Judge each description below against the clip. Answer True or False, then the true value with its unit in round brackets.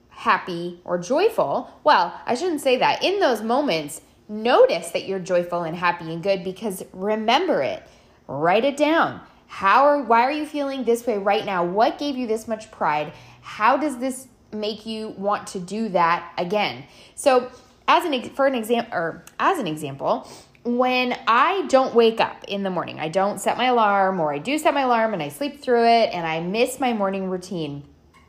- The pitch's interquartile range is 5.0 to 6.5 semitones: True (5.6 semitones)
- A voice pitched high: True (220 Hz)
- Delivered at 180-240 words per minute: True (195 wpm)